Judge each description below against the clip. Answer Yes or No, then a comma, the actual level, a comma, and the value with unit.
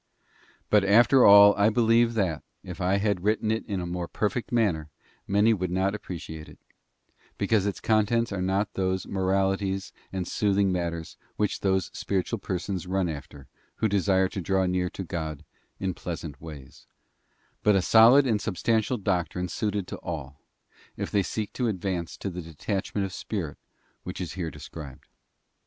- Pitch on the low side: Yes, very low, 95 Hz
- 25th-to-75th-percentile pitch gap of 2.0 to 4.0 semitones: Yes, average, 2.9 semitones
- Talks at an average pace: Yes, average, 165 wpm